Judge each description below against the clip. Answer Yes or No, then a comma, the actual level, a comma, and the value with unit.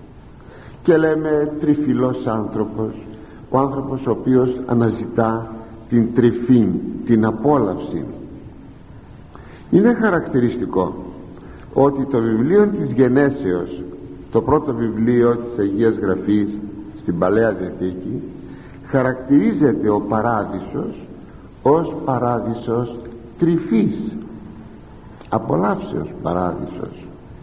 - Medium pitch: No, low, 115 Hz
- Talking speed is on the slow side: Yes, slow, 80 wpm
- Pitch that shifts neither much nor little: Yes, average, 3.6 semitones